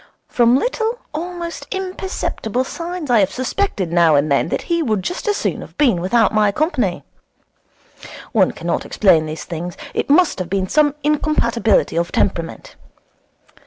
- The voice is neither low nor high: No, high, 240 Hz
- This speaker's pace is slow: No, average, 155 wpm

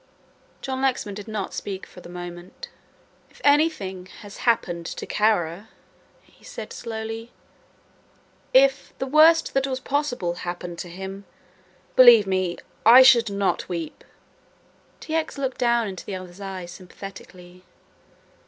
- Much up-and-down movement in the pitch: Yes, wide, 6.1 semitones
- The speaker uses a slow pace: Yes, slow, 130 wpm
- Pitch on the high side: Yes, high, 205 Hz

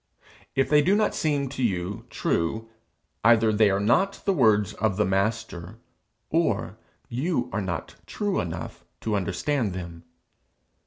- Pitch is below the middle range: Yes, low, 110 Hz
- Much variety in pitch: Yes, wide, 6.3 semitones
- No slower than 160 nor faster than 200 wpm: No, average, 145 wpm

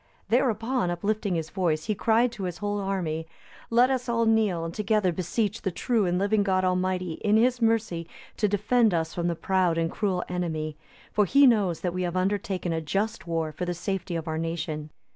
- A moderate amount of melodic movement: Yes, average, 4.2 semitones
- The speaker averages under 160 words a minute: No, average, 200 wpm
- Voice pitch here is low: No, medium, 185 Hz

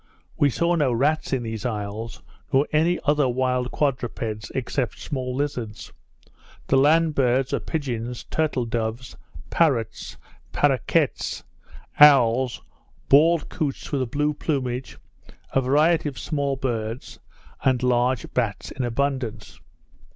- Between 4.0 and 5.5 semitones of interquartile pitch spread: No, average, 3.4 semitones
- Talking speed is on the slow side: Yes, slow, 120 wpm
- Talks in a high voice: No, low, 130 Hz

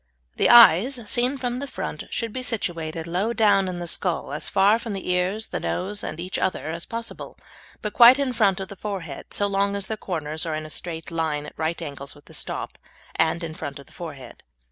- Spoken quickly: Yes, fast, 225 wpm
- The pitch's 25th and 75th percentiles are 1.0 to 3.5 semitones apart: No, average, 5.2 semitones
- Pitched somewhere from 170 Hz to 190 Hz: Yes, medium, 185 Hz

